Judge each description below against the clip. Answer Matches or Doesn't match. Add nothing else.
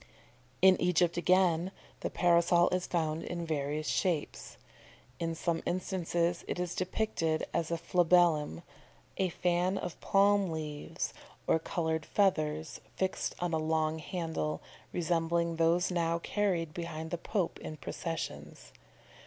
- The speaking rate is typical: Doesn't match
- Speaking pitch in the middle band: Matches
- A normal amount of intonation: Doesn't match